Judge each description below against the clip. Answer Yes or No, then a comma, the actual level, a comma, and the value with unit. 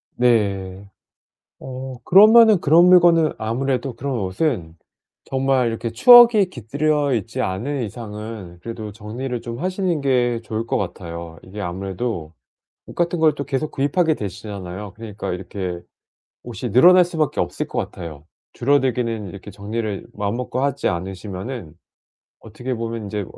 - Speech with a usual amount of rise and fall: No, wide, 5.9 semitones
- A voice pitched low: Yes, low, 115 Hz